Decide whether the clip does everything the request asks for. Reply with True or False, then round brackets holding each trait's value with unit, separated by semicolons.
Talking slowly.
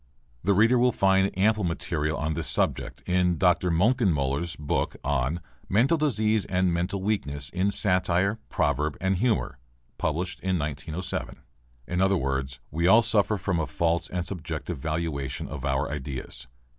False (150 wpm)